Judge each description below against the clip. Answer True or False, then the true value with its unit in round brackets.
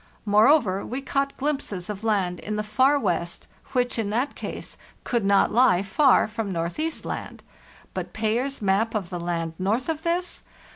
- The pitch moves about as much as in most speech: False (5.8 semitones)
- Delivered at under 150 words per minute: False (165 wpm)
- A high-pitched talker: True (220 Hz)